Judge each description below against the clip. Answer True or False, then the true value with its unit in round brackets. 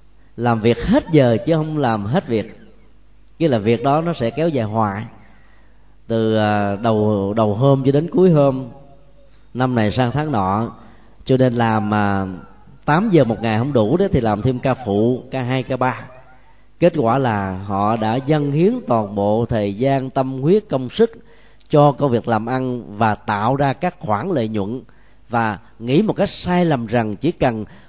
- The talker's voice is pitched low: True (125 Hz)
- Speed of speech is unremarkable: True (185 wpm)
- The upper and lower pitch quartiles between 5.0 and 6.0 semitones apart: False (4.1 semitones)